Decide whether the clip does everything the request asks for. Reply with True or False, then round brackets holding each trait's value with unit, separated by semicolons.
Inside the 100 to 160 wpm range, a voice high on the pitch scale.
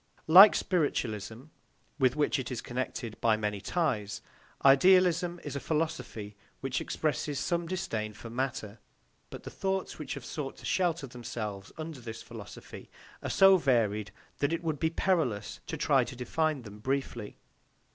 False (155 wpm; 135 Hz)